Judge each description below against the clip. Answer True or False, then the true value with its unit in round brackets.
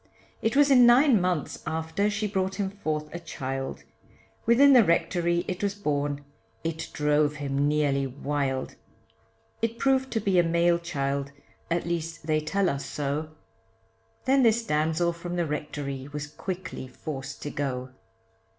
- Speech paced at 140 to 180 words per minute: True (150 wpm)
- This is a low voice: False (165 Hz)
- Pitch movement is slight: False (5.1 semitones)